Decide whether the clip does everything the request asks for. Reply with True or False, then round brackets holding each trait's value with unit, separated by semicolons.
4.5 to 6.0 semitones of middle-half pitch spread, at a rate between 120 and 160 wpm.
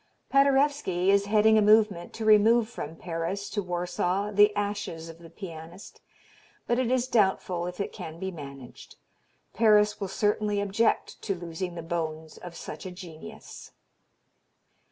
False (3.8 semitones; 150 wpm)